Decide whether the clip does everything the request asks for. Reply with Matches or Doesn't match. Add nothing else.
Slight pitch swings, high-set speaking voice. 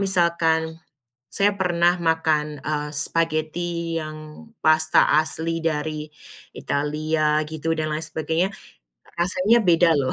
Doesn't match